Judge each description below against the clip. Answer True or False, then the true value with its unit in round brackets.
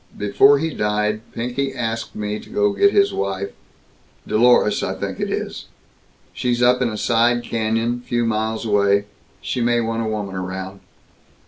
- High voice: False (115 Hz)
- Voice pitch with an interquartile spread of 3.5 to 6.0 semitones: False (2.7 semitones)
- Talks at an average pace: True (160 wpm)